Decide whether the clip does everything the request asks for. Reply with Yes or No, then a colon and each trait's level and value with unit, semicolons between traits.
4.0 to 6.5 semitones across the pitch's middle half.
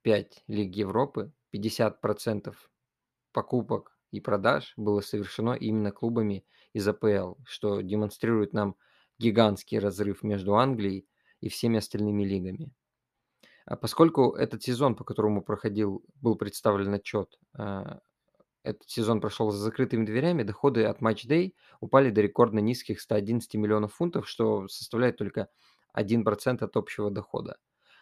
No: narrow, 2.4 semitones